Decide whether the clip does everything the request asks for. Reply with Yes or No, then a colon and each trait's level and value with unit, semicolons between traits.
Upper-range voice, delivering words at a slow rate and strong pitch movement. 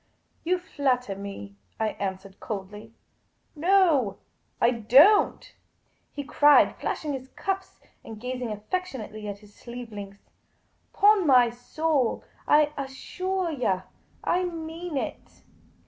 Yes: very high, 255 Hz; slow, 125 wpm; wide, 7.4 semitones